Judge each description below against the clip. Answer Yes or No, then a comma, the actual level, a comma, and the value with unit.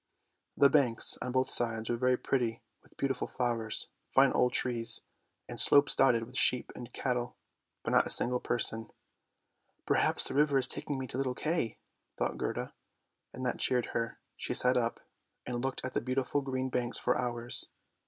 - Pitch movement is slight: Yes, narrow, 1.9 semitones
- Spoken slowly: No, average, 180 wpm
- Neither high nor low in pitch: No, low, 125 Hz